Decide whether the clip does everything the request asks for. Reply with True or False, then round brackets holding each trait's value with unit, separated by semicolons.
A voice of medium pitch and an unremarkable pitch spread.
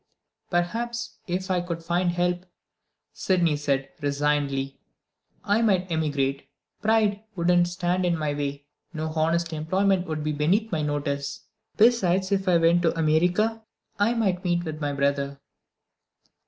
True (170 Hz; 4.0 semitones)